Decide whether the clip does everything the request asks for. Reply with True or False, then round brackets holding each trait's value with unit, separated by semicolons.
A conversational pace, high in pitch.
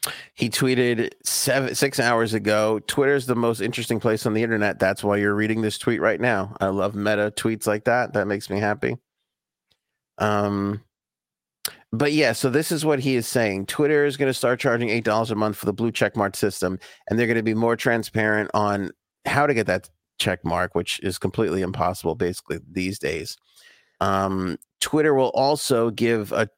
False (190 wpm; 110 Hz)